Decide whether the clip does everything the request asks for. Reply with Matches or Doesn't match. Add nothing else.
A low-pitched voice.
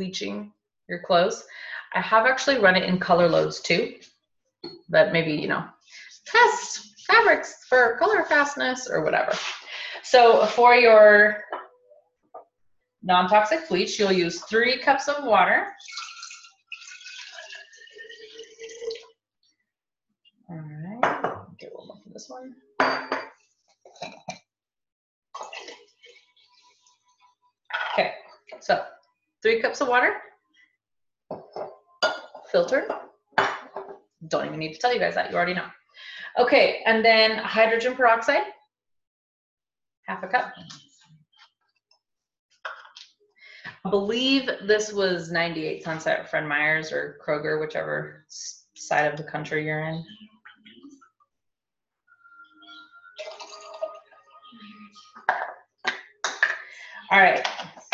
Doesn't match